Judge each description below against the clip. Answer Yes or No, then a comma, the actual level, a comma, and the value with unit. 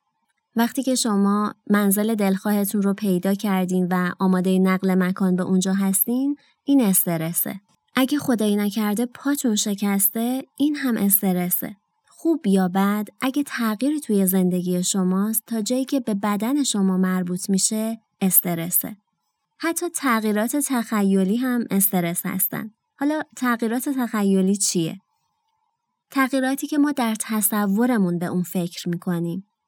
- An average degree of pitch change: Yes, average, 4.8 semitones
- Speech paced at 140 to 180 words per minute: No, average, 125 wpm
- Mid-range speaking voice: No, high, 210 Hz